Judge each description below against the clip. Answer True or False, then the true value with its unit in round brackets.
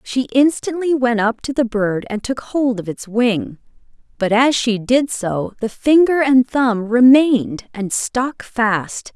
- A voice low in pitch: False (240 Hz)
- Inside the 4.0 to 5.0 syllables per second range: False (3.7 syllables/s)